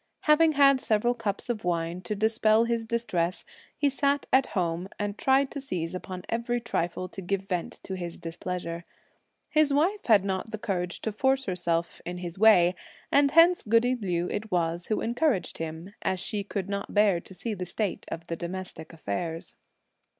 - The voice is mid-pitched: No, high, 200 Hz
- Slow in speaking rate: No, average, 180 wpm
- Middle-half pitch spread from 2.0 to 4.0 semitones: No, average, 5.1 semitones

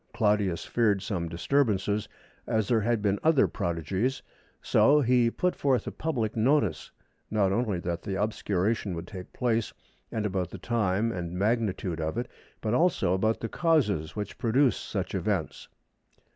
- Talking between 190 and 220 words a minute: No, average, 155 wpm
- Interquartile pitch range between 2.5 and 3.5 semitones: No, average, 4.1 semitones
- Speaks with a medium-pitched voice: No, low, 105 Hz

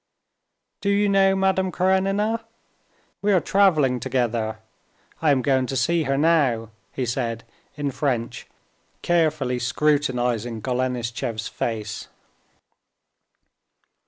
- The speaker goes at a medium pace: No, slow, 100 wpm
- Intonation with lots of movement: Yes, wide, 6.3 semitones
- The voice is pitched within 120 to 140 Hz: Yes, low, 135 Hz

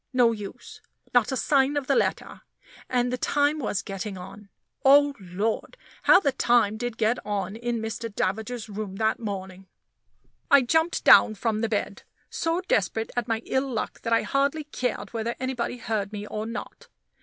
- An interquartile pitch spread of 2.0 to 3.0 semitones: No, average, 3.7 semitones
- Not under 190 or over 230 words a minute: No, average, 175 wpm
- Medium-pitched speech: No, high, 230 Hz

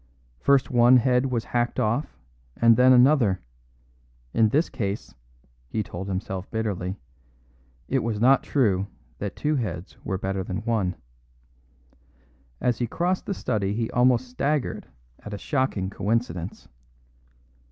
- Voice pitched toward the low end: Yes, low, 115 Hz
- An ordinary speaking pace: No, slow, 130 wpm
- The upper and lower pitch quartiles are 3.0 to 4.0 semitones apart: No, average, 4.6 semitones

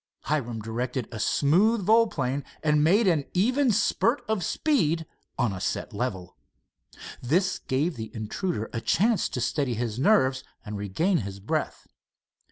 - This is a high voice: No, medium, 145 Hz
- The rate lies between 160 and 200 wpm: No, average, 145 wpm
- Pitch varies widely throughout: Yes, wide, 8.8 semitones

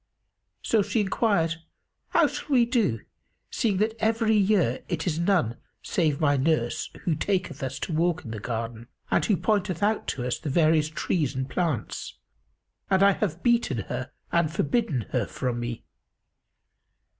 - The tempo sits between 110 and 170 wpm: Yes, average, 160 wpm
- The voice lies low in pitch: No, medium, 170 Hz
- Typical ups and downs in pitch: No, wide, 6.8 semitones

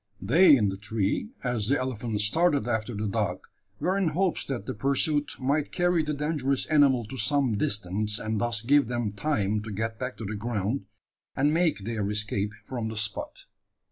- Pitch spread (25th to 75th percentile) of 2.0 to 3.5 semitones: No, wide, 5.4 semitones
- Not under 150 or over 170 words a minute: No, average, 185 wpm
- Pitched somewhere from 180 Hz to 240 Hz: No, low, 120 Hz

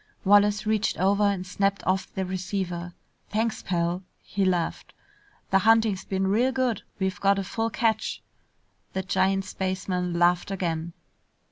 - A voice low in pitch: No, high, 190 Hz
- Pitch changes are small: Yes, narrow, 2.1 semitones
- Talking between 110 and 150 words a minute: Yes, average, 140 wpm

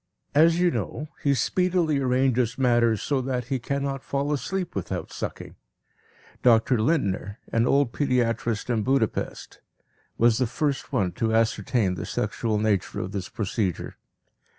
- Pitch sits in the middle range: No, low, 125 Hz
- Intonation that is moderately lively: Yes, average, 3.9 semitones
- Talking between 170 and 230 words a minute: No, average, 140 wpm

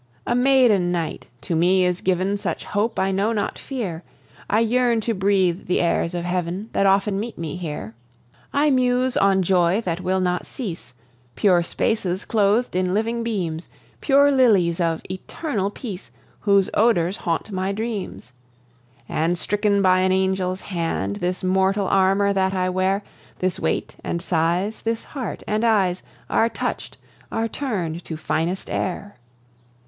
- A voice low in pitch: No, high, 190 Hz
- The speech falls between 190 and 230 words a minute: No, average, 155 wpm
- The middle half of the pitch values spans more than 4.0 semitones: No, average, 3.4 semitones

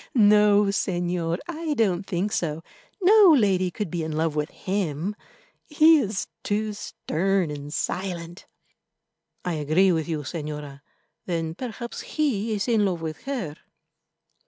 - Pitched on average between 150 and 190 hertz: Yes, medium, 185 Hz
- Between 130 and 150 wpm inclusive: Yes, slow, 135 wpm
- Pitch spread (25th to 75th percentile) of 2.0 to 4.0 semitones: No, average, 4.6 semitones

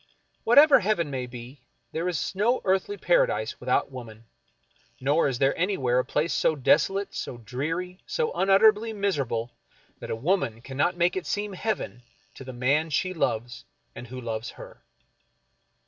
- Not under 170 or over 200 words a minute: No, average, 155 wpm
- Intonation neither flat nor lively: No, wide, 7.6 semitones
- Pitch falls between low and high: Yes, medium, 155 Hz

